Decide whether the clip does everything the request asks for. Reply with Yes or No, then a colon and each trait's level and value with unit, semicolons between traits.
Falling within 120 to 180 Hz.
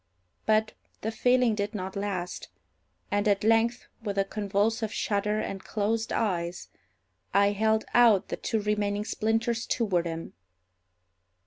No: high, 210 Hz